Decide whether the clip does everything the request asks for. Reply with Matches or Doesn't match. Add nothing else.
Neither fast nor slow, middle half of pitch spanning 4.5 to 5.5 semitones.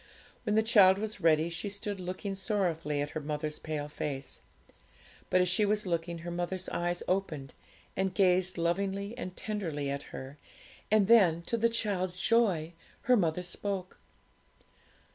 Doesn't match